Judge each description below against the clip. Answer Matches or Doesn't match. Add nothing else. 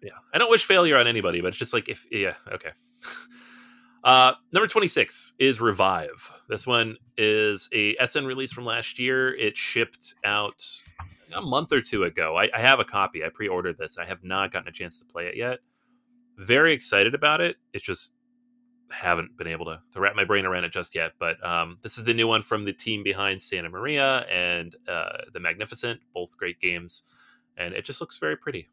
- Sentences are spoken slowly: Doesn't match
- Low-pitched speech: Matches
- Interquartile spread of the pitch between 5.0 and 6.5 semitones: Matches